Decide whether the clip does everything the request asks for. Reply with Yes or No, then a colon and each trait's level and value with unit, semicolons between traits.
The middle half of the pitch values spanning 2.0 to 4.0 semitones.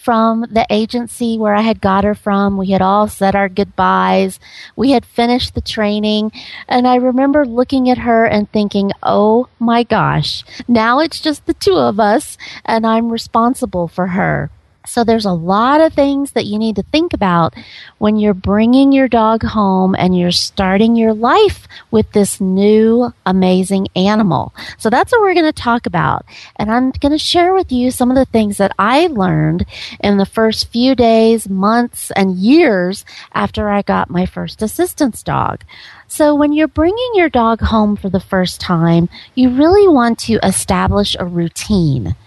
No: average, 4.4 semitones